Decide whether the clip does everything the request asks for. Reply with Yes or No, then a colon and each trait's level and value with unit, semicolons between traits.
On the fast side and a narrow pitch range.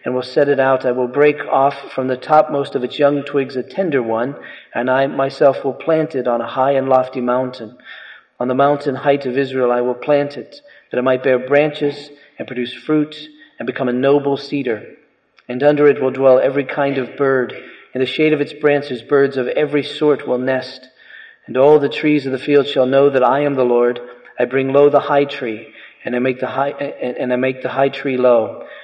Yes: fast, 225 wpm; narrow, 2.1 semitones